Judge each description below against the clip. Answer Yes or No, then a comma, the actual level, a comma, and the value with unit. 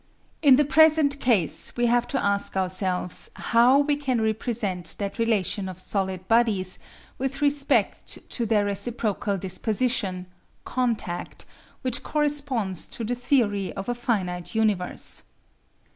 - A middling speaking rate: No, slow, 130 wpm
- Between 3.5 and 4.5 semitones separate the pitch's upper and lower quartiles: No, average, 4.9 semitones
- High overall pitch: Yes, high, 225 Hz